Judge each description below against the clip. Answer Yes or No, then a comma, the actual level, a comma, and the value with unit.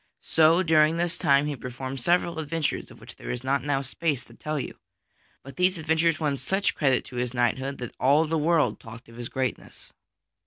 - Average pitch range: Yes, average, 3.7 semitones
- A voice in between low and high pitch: Yes, medium, 145 Hz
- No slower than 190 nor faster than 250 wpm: Yes, average, 200 wpm